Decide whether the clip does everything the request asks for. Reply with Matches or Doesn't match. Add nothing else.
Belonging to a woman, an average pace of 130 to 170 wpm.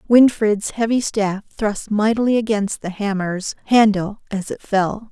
Matches